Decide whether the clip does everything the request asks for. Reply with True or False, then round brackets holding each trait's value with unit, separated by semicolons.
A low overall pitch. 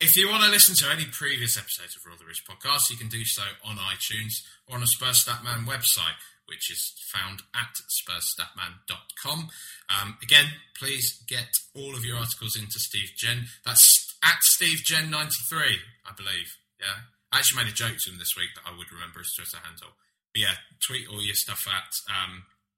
True (115 Hz)